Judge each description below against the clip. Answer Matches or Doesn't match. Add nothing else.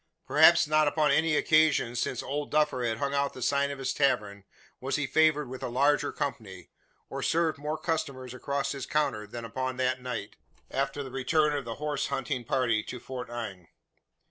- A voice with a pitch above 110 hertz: Matches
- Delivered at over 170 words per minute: Matches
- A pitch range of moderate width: Matches